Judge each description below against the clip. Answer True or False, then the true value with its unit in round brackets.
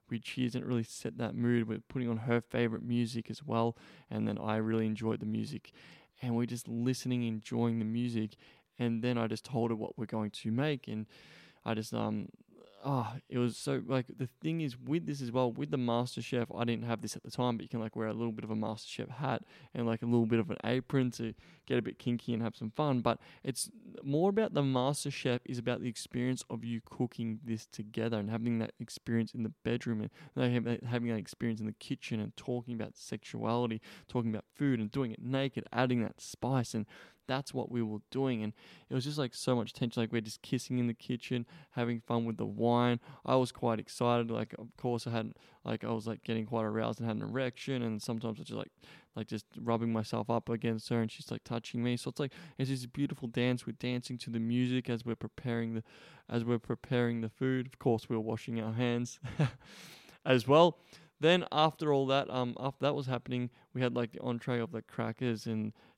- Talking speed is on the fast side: True (230 wpm)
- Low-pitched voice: True (120 Hz)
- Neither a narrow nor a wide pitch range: False (2.1 semitones)